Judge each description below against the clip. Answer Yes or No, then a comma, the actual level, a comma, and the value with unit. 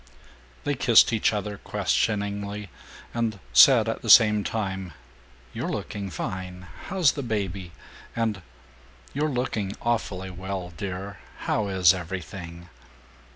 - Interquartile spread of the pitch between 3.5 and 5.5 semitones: No, average, 3.0 semitones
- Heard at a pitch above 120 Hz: No, low, 100 Hz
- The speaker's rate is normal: No, slow, 115 wpm